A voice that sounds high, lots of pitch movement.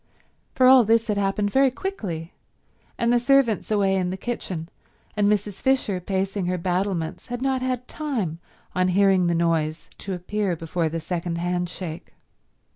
No: high, 195 Hz; average, 4.8 semitones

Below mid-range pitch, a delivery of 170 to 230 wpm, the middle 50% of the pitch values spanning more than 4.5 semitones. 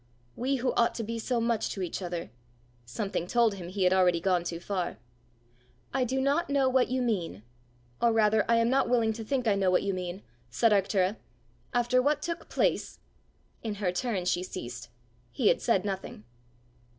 No: high, 210 Hz; average, 200 wpm; average, 5.0 semitones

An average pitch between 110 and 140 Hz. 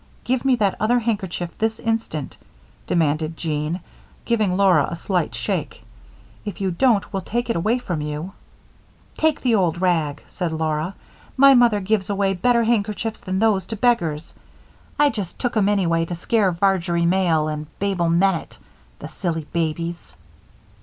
No: high, 190 Hz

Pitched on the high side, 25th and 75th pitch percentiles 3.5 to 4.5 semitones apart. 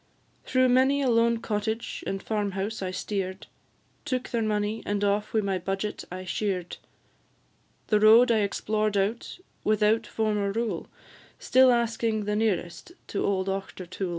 No: high, 210 Hz; narrow, 2.6 semitones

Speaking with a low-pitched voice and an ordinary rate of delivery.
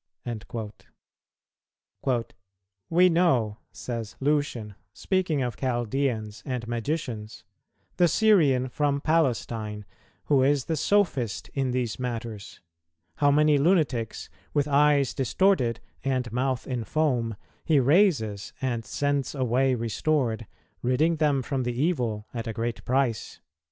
No: low, 130 Hz; slow, 115 wpm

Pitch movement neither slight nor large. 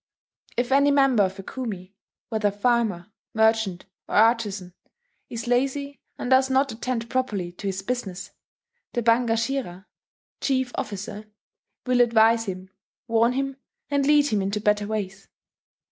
Yes: average, 4.0 semitones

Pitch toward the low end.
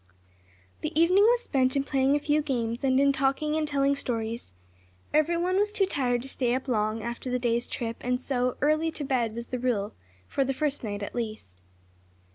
No: very high, 265 Hz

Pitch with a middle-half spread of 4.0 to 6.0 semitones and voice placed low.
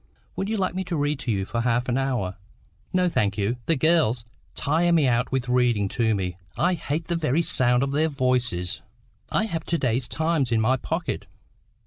Yes: wide, 5.6 semitones; low, 130 Hz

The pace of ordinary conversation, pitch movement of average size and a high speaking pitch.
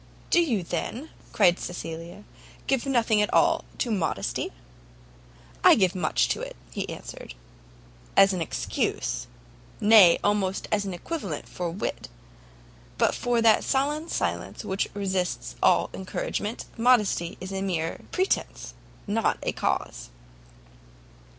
No: slow, 125 wpm; average, 4.9 semitones; high, 200 Hz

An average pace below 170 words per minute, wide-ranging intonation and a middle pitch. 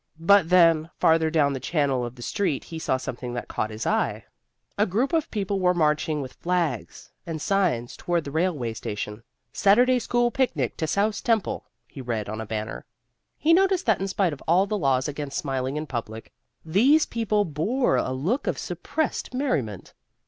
No: average, 185 wpm; wide, 7.6 semitones; medium, 160 Hz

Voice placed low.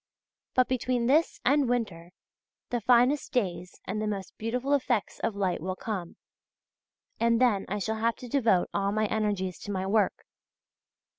No: high, 220 Hz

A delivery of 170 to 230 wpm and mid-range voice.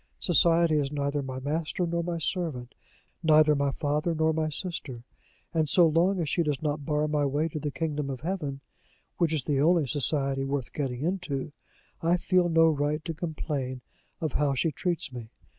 Yes: average, 185 wpm; medium, 150 Hz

